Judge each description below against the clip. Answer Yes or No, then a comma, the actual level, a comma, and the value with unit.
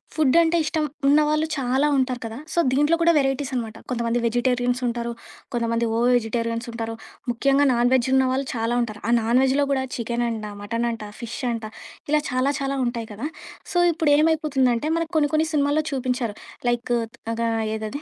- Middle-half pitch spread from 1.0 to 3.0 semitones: No, average, 3.6 semitones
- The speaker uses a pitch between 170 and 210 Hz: No, very high, 250 Hz